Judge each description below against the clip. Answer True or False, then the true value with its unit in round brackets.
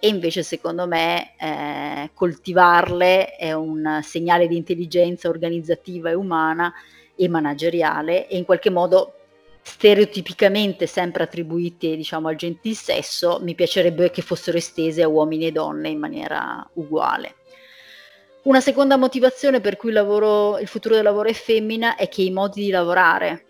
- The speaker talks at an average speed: True (150 wpm)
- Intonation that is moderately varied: True (3.5 semitones)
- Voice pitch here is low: False (180 Hz)